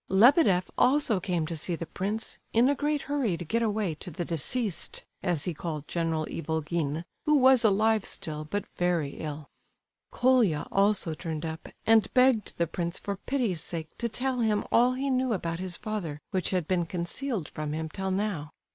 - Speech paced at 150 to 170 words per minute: No, average, 180 wpm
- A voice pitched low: No, medium, 185 Hz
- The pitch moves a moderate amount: No, wide, 5.8 semitones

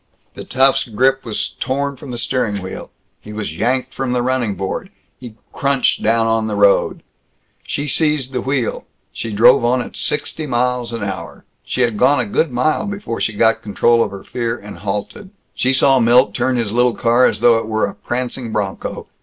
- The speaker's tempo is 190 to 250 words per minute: Yes, average, 195 wpm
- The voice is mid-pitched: No, low, 120 Hz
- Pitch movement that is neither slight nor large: Yes, average, 3.0 semitones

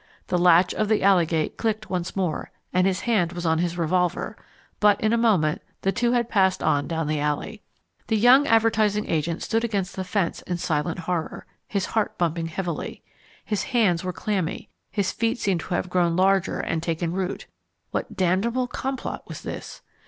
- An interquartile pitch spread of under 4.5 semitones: Yes, average, 4.1 semitones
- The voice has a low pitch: No, medium, 185 Hz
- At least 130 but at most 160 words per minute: No, average, 185 wpm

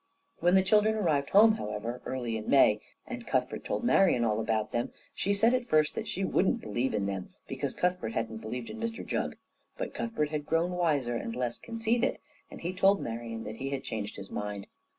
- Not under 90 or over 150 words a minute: No, fast, 205 wpm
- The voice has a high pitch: No, medium, 140 Hz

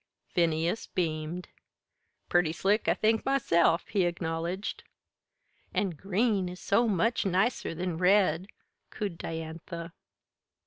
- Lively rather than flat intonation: No, average, 3.4 semitones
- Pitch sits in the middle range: Yes, medium, 180 Hz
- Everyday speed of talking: No, slow, 105 wpm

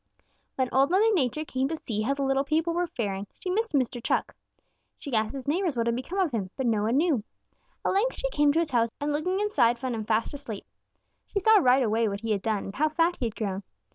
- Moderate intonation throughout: No, wide, 6.4 semitones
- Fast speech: Yes, fast, 250 wpm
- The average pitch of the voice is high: Yes, very high, 270 Hz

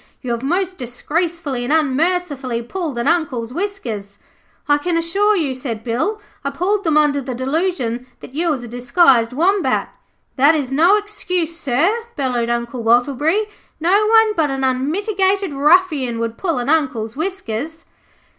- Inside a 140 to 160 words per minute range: Yes, average, 155 wpm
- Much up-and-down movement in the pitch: Yes, wide, 6.2 semitones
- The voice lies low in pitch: No, very high, 295 Hz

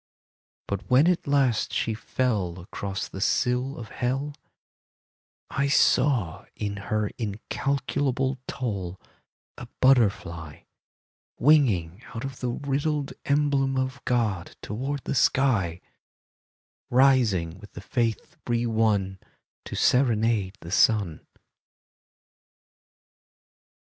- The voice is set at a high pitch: No, low, 120 Hz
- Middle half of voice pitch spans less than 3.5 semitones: No, average, 5.1 semitones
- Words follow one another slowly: Yes, slow, 105 wpm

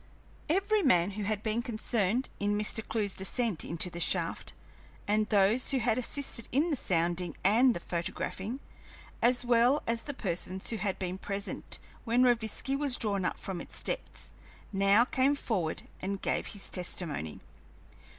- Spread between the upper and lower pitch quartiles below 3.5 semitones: No, average, 4.4 semitones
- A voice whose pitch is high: Yes, high, 215 Hz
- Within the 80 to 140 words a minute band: No, average, 160 wpm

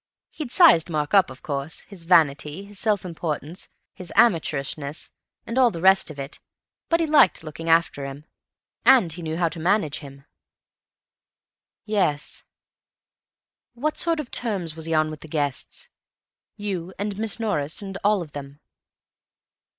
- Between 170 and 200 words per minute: No, average, 145 wpm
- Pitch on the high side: No, medium, 170 Hz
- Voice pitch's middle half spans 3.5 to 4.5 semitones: No, wide, 5.4 semitones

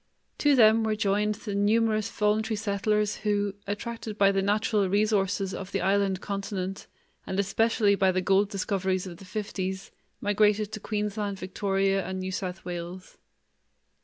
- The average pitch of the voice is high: Yes, high, 200 Hz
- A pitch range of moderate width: No, narrow, 1.6 semitones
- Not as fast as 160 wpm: Yes, average, 150 wpm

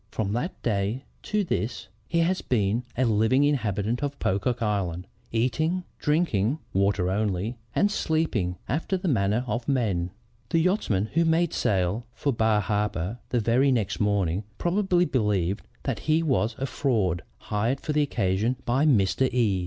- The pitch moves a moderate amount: No, wide, 6.2 semitones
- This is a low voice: Yes, low, 115 Hz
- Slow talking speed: No, average, 155 wpm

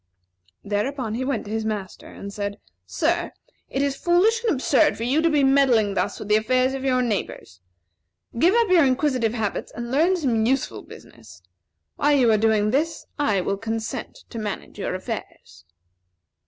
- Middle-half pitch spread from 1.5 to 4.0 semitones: No, average, 4.7 semitones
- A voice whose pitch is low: No, very high, 250 Hz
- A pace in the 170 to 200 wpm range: Yes, average, 175 wpm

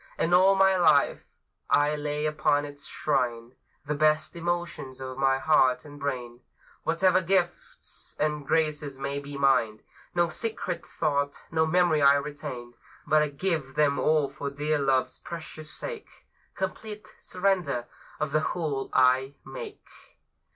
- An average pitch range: Yes, average, 3.4 semitones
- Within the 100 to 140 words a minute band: Yes, slow, 135 wpm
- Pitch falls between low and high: Yes, medium, 150 Hz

